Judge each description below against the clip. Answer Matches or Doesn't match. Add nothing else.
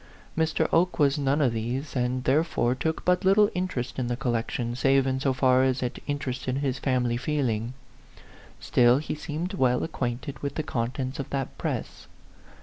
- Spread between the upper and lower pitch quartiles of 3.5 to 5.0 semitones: Doesn't match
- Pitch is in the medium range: Doesn't match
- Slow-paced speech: Doesn't match